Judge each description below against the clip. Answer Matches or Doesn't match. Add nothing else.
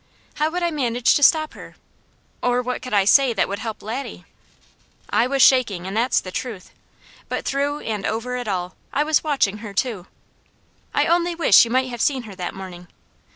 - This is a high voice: Matches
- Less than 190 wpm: Doesn't match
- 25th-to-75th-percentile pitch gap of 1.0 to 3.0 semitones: Doesn't match